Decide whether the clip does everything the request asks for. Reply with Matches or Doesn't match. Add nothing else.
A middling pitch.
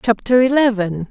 Doesn't match